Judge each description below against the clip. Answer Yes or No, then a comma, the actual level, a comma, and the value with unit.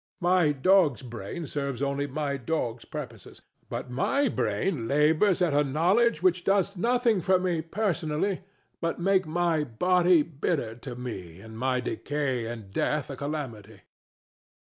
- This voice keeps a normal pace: Yes, average, 145 wpm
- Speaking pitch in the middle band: Yes, medium, 150 Hz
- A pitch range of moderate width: No, wide, 6.0 semitones